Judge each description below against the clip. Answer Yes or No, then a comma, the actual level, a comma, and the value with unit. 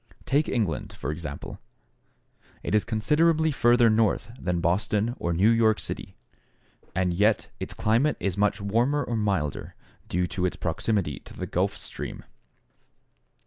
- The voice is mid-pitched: No, low, 105 Hz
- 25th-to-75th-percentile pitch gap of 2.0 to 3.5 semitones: No, average, 4.6 semitones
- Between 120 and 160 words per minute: Yes, average, 145 wpm